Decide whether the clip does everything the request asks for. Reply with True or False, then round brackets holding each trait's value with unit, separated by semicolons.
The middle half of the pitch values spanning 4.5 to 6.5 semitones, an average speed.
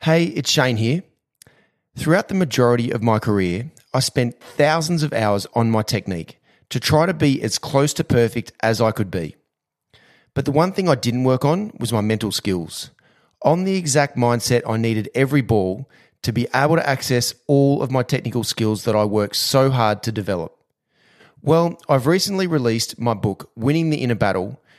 True (4.9 semitones; 185 wpm)